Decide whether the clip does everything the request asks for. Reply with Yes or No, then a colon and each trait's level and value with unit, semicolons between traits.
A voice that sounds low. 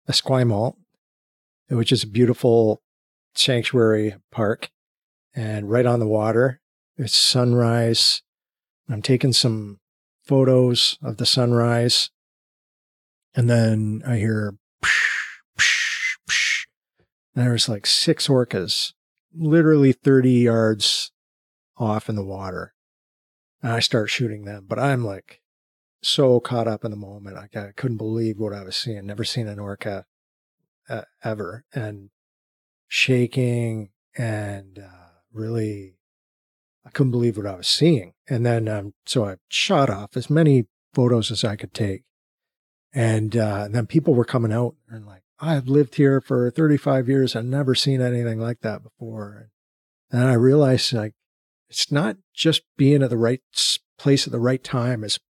Yes: low, 115 Hz